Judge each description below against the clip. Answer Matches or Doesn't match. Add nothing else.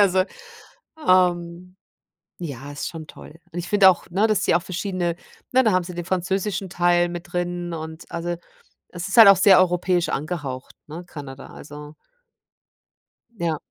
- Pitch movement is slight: Matches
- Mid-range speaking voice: Matches